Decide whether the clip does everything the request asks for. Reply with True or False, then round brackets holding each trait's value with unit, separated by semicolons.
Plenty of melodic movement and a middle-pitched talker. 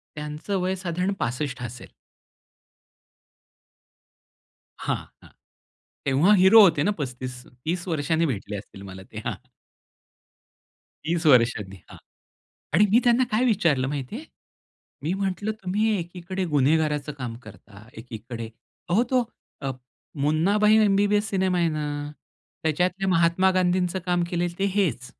True (6.2 semitones; 170 Hz)